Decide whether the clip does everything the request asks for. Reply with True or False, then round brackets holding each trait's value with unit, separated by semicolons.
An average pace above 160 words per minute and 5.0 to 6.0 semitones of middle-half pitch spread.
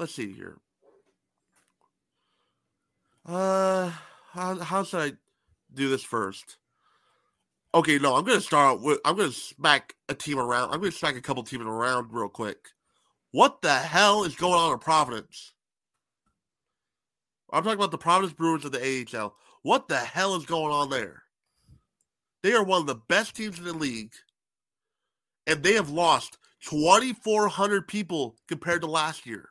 False (155 wpm; 5.5 semitones)